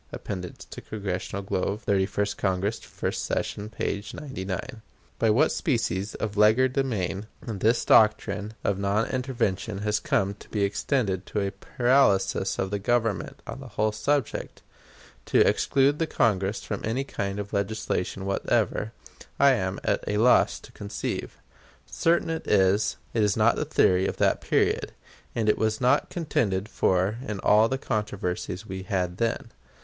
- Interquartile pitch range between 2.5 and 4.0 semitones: Yes, average, 3.0 semitones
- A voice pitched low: Yes, low, 105 Hz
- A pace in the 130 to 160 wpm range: Yes, average, 155 wpm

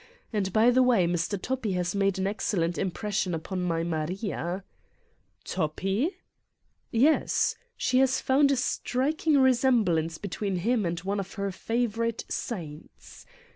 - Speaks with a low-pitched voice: No, high, 200 Hz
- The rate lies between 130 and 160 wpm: Yes, average, 140 wpm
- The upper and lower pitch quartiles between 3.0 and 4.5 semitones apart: No, wide, 5.6 semitones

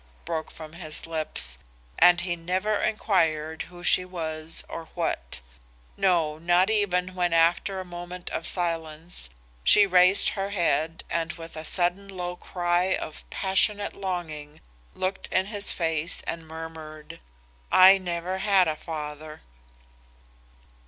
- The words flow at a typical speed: No, slow, 130 wpm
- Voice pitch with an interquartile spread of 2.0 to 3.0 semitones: Yes, average, 2.7 semitones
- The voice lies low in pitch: No, medium, 175 Hz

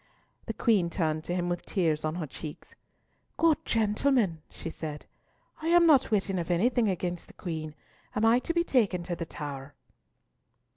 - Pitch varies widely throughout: Yes, wide, 6.2 semitones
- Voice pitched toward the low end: No, medium, 180 Hz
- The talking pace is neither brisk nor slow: Yes, average, 175 wpm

